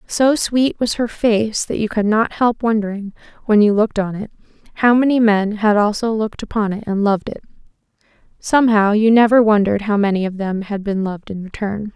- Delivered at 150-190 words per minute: No, average, 200 wpm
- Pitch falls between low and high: No, high, 215 Hz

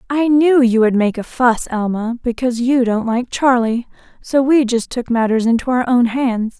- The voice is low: No, high, 240 Hz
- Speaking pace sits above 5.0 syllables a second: No, 4.7 syllables/s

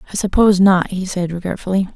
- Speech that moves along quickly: No, average, 185 wpm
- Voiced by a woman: Yes, female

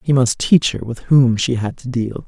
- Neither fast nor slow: No, fast, 265 wpm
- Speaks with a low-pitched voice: Yes, low, 125 Hz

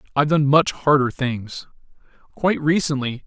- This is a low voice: No, medium, 145 Hz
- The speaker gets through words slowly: Yes, slow, 130 wpm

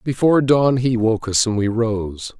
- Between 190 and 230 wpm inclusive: Yes, average, 200 wpm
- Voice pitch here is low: Yes, low, 115 Hz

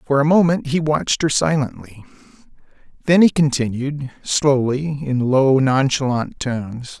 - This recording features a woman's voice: No, male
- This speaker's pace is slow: Yes, slow, 130 wpm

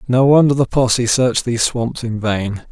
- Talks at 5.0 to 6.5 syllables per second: No, 4.7 syllables/s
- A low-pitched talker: Yes, low, 120 Hz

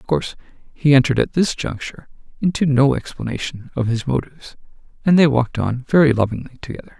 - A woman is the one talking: No, male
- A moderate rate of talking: Yes, average, 170 wpm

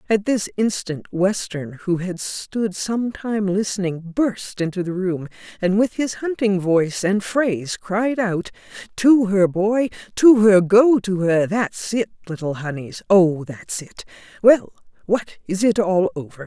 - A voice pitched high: Yes, high, 195 Hz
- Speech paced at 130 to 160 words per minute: Yes, average, 155 wpm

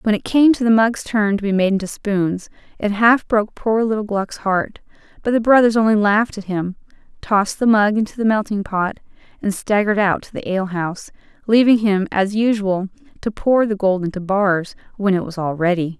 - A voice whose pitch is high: Yes, high, 205 Hz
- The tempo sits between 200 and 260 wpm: Yes, fast, 205 wpm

